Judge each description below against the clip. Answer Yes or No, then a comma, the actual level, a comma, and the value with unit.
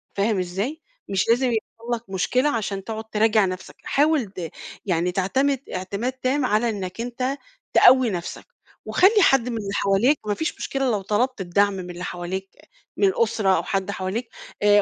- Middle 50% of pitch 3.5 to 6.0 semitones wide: Yes, average, 4.8 semitones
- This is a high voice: Yes, high, 215 Hz